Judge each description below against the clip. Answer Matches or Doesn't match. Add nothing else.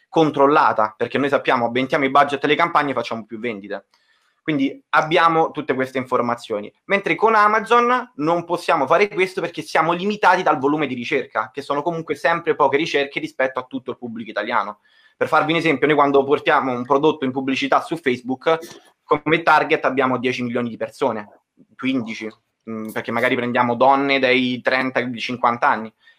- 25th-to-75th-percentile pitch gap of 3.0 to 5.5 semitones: Matches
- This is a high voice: Doesn't match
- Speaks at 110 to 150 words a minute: Doesn't match